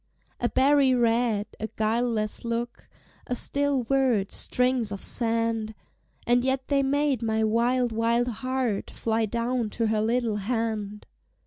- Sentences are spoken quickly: No, slow, 135 wpm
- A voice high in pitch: Yes, high, 235 Hz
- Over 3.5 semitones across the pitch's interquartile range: No, narrow, 2.4 semitones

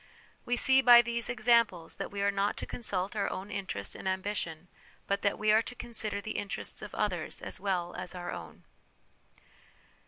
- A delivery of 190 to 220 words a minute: Yes, average, 195 wpm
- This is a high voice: Yes, high, 200 Hz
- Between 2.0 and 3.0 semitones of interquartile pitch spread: No, average, 3.5 semitones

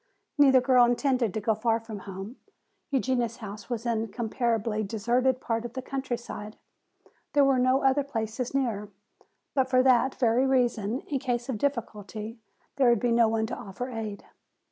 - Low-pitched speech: No, high, 240 Hz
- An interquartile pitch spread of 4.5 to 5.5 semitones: No, average, 2.8 semitones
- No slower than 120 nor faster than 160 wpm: No, average, 170 wpm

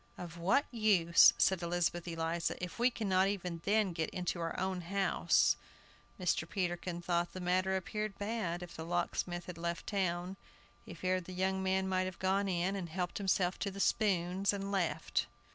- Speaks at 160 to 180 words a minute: Yes, average, 175 wpm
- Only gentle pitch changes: Yes, narrow, 2.0 semitones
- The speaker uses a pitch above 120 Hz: Yes, medium, 185 Hz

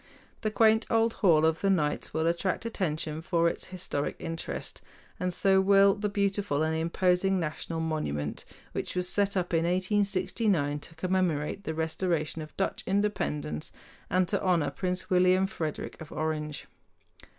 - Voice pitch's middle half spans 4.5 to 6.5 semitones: No, average, 3.5 semitones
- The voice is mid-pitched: Yes, medium, 180 Hz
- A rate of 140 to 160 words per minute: Yes, average, 150 wpm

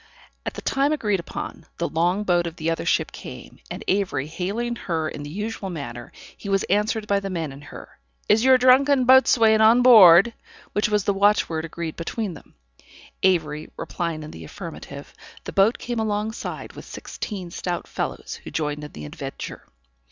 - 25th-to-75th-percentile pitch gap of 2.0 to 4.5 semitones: No, average, 5.1 semitones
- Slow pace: No, average, 180 wpm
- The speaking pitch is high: Yes, high, 195 Hz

